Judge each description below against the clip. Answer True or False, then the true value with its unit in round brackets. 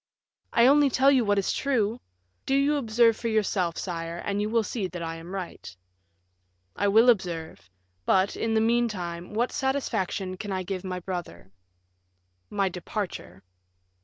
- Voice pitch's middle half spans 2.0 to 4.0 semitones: False (4.6 semitones)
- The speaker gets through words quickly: False (160 wpm)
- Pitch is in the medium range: False (200 Hz)